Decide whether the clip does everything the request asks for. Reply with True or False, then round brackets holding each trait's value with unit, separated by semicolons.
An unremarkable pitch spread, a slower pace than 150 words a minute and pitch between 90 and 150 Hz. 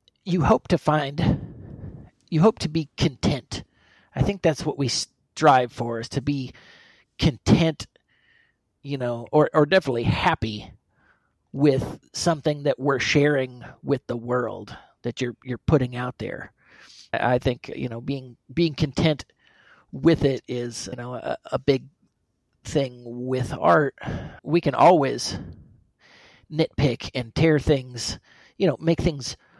True (3.9 semitones; 140 wpm; 135 Hz)